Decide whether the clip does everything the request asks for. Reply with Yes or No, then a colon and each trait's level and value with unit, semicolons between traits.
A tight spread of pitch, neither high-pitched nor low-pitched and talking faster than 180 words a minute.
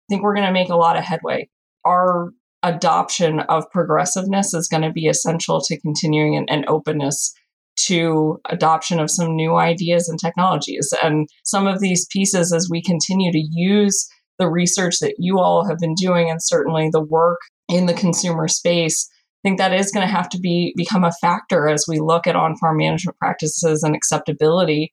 Yes: narrow, 2.2 semitones; medium, 170 Hz; average, 190 wpm